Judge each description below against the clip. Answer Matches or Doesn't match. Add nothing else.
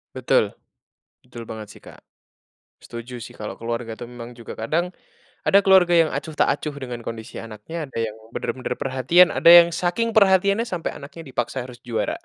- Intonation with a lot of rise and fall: Matches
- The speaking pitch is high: Doesn't match